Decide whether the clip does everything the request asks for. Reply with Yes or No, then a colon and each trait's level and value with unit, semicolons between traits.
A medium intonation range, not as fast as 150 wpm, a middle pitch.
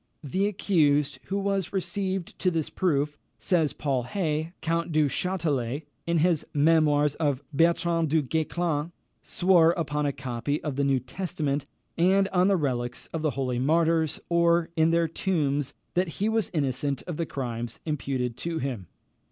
No: average, 3.3 semitones; average, 160 wpm; medium, 155 Hz